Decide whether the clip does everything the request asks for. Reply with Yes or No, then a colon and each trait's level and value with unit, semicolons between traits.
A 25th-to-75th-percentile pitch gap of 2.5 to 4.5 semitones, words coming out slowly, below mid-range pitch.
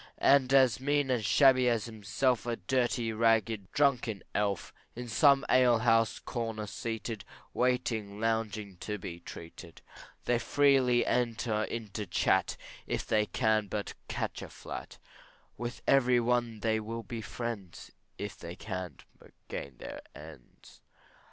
Yes: average, 2.9 semitones; slow, 130 wpm; low, 115 Hz